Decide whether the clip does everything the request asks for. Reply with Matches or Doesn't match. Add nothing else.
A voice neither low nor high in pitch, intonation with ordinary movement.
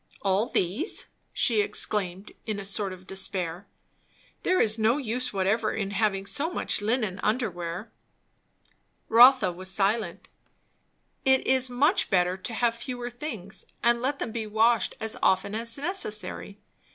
Doesn't match